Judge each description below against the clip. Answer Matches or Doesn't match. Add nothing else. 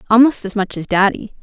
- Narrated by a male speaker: Doesn't match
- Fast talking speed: Matches